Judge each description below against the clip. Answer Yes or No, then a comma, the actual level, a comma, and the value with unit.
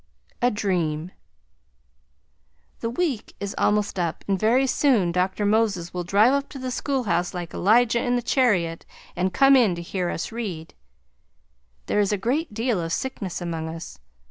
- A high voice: Yes, high, 205 Hz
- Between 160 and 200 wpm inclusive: Yes, average, 170 wpm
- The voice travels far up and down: Yes, wide, 5.7 semitones